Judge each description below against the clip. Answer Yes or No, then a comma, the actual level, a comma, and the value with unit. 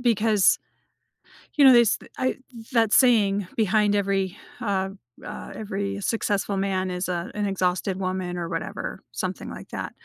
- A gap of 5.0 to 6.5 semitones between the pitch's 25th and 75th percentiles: No, narrow, 2.4 semitones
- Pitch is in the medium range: No, high, 200 Hz